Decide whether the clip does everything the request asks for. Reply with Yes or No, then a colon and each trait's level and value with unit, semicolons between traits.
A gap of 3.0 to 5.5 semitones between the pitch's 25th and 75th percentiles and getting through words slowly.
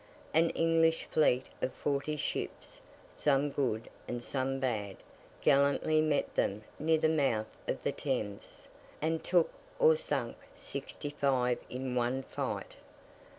Yes: average, 3.9 semitones; slow, 130 wpm